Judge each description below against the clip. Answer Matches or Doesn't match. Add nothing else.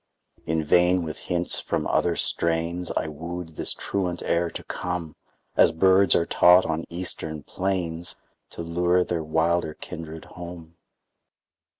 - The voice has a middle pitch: Doesn't match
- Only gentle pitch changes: Matches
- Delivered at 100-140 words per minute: Matches